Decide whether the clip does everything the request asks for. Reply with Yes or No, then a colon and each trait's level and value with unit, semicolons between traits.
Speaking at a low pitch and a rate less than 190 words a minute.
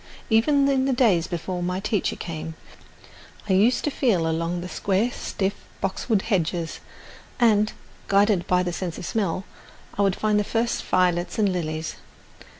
No: high, 195 Hz; average, 150 wpm